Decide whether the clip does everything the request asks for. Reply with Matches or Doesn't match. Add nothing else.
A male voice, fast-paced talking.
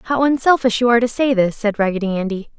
Doesn't match